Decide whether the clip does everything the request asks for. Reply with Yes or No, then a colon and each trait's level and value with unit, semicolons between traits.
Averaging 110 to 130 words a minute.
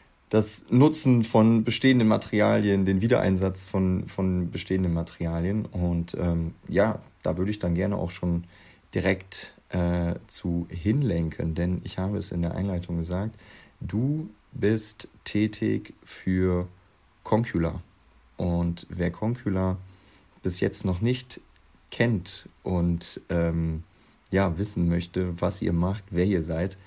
Yes: slow, 125 wpm